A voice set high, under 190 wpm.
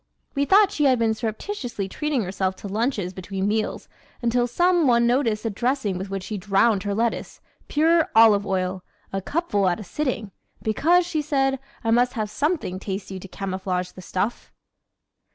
Yes: high, 220 Hz; average, 170 wpm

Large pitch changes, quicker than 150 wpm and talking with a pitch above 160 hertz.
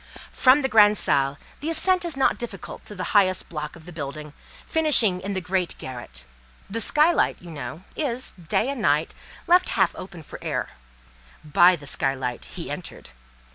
Yes: wide, 9.0 semitones; average, 170 wpm; medium, 185 Hz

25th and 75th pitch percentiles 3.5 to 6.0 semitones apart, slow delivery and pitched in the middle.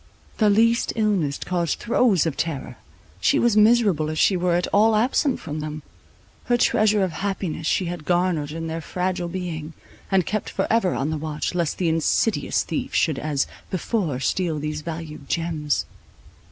No: average, 4.7 semitones; average, 165 wpm; medium, 175 Hz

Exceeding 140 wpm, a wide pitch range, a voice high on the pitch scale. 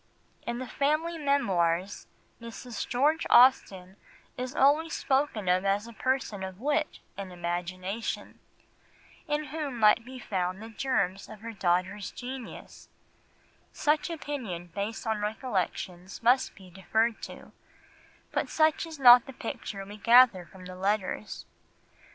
No: slow, 135 wpm; wide, 5.8 semitones; high, 225 Hz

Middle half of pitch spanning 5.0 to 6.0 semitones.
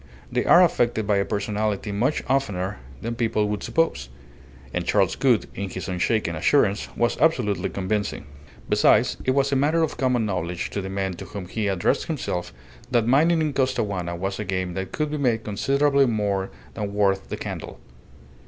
Yes: average, 5.3 semitones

